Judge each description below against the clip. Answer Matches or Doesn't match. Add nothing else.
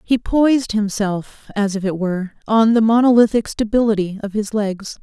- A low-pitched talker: Doesn't match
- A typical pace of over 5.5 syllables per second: Doesn't match